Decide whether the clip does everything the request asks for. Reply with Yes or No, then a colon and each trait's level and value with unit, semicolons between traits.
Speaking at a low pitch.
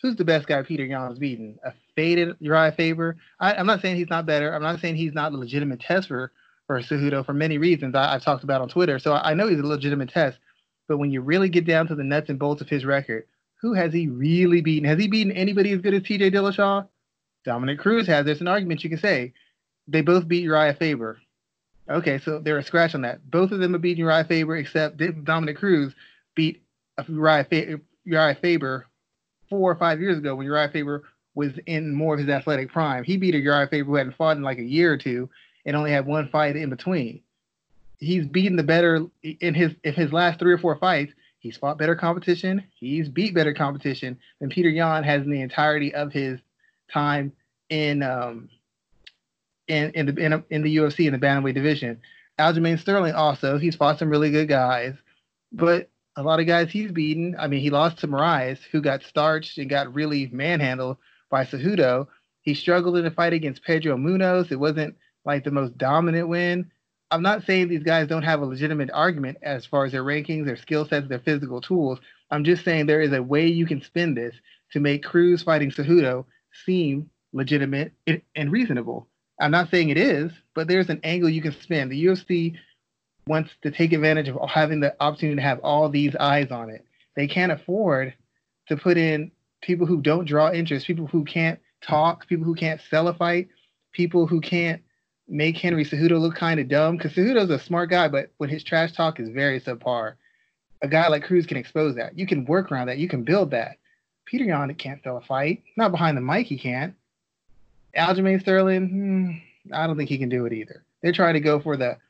No: medium, 155 Hz